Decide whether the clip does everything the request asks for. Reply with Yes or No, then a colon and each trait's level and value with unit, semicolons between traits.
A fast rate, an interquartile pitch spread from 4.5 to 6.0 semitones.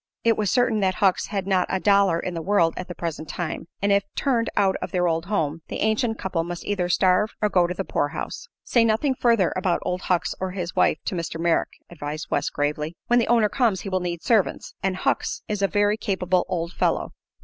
No: fast, 225 wpm; average, 3.4 semitones